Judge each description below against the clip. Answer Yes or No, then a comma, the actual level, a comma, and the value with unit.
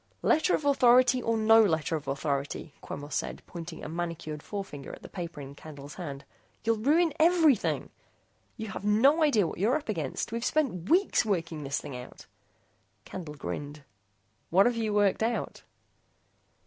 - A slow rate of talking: No, average, 160 wpm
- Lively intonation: Yes, wide, 7.9 semitones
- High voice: Yes, high, 195 Hz